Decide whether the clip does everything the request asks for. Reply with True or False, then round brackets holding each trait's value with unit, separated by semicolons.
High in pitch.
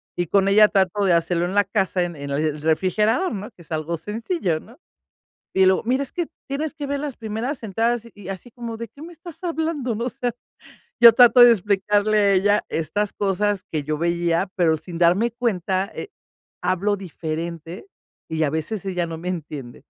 True (200 Hz)